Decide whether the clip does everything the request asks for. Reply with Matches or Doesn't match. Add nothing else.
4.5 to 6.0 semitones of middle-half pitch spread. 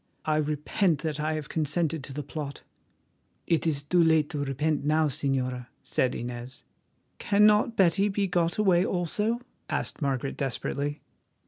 Doesn't match